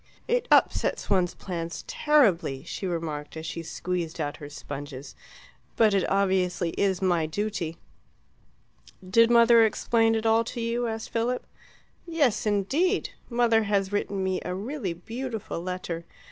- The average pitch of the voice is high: Yes, high, 195 Hz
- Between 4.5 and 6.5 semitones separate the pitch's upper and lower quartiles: Yes, average, 5.2 semitones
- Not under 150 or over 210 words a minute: No, average, 140 wpm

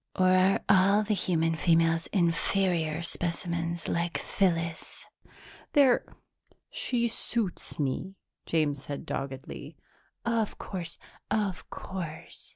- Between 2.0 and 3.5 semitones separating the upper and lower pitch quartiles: Yes, average, 3.1 semitones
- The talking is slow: Yes, slow, 100 wpm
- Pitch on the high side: No, medium, 170 Hz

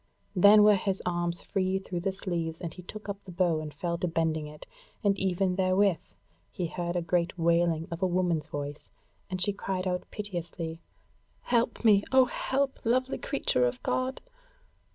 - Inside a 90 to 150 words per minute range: No, average, 175 wpm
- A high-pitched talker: No, medium, 180 Hz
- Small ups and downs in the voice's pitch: No, average, 3.0 semitones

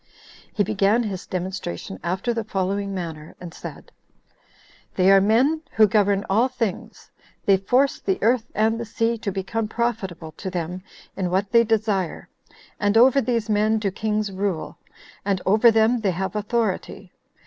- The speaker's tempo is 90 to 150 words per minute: No, average, 160 wpm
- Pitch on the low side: No, high, 205 Hz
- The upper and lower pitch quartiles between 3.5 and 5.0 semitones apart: No, average, 3.0 semitones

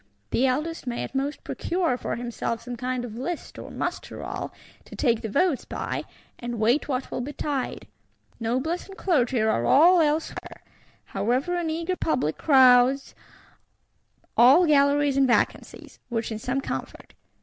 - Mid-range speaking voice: No, very high, 265 Hz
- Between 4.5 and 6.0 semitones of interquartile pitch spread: No, average, 4.1 semitones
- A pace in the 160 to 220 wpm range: No, average, 150 wpm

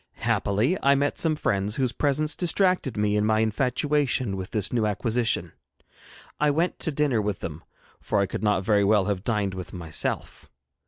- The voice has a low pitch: Yes, low, 110 Hz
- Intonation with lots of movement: Yes, wide, 5.8 semitones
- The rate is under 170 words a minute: No, average, 175 wpm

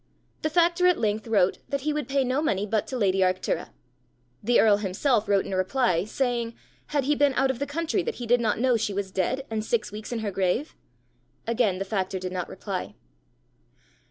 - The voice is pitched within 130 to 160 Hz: No, high, 225 Hz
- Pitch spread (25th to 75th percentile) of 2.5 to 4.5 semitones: No, wide, 5.5 semitones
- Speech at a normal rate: No, fast, 210 wpm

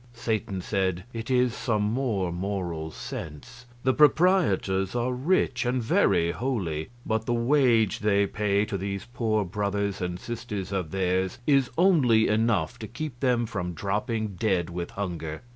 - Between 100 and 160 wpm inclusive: Yes, average, 150 wpm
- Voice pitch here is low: Yes, low, 105 Hz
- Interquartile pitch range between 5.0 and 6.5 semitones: No, average, 4.3 semitones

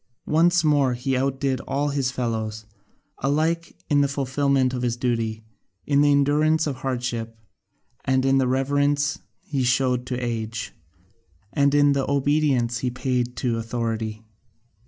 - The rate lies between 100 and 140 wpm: Yes, slow, 135 wpm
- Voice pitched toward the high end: No, low, 130 Hz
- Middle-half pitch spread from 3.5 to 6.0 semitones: No, average, 2.8 semitones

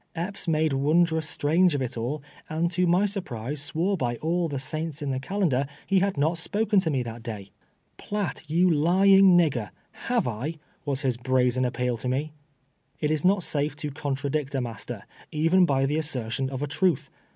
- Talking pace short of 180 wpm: No, average, 195 wpm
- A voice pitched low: No, medium, 150 Hz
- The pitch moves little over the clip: No, average, 4.8 semitones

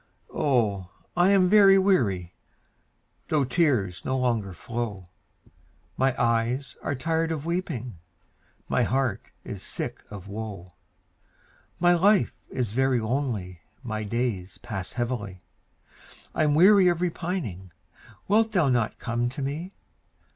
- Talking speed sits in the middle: No, slow, 120 wpm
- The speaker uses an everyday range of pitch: No, wide, 7.5 semitones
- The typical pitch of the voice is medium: No, low, 125 Hz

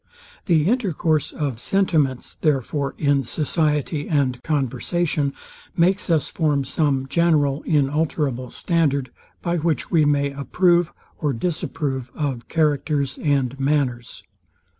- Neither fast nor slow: No, slow, 110 wpm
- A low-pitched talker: No, medium, 145 Hz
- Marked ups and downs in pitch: No, average, 3.0 semitones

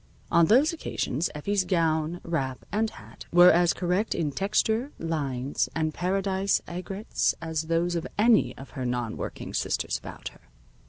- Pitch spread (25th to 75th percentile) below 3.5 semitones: No, average, 3.9 semitones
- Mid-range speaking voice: Yes, medium, 170 Hz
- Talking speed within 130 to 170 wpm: Yes, average, 155 wpm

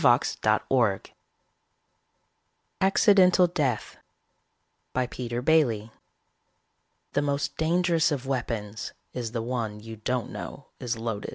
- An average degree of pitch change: No, wide, 5.8 semitones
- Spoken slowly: Yes, slow, 100 wpm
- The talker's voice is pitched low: Yes, low, 125 Hz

